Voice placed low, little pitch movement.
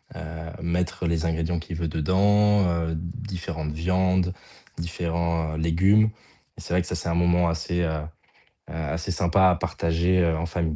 Yes: very low, 85 Hz; narrow, 1.7 semitones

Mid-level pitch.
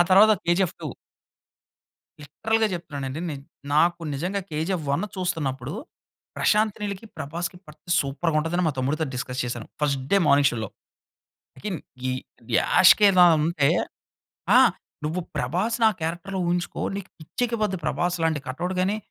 Yes: medium, 170 Hz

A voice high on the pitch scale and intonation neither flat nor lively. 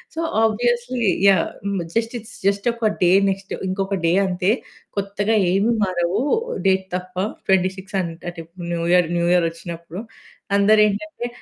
Yes: high, 195 Hz; average, 3.0 semitones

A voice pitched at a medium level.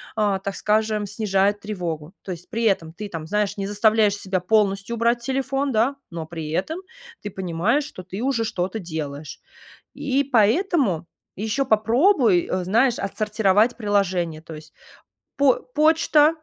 No: high, 210 Hz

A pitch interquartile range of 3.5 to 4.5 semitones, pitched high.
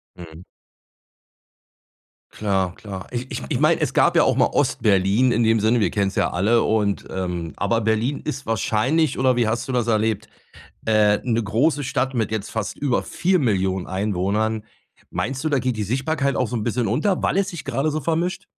No: average, 4.2 semitones; low, 115 Hz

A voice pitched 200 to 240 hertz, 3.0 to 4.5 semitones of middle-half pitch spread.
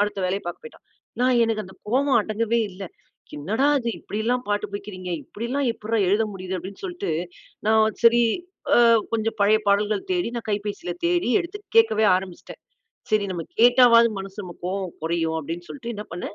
Yes: high, 210 Hz; average, 3.7 semitones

